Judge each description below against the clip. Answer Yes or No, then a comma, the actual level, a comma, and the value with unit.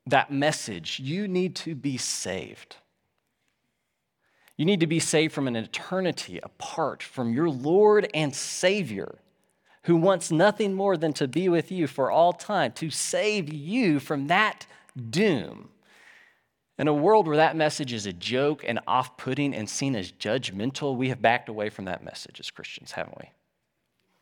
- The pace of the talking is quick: No, average, 165 wpm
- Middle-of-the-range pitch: Yes, medium, 150 Hz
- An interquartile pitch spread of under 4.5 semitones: No, wide, 5.5 semitones